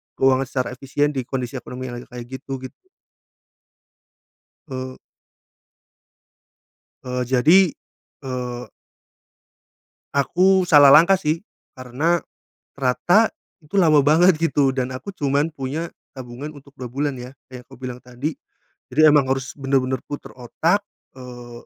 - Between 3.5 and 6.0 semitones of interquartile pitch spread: No, average, 3.1 semitones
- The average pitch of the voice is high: No, low, 135 Hz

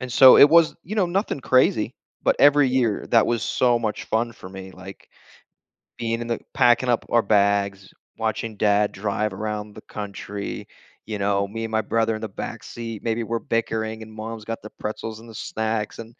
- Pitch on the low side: Yes, low, 110 Hz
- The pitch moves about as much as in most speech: No, narrow, 2.0 semitones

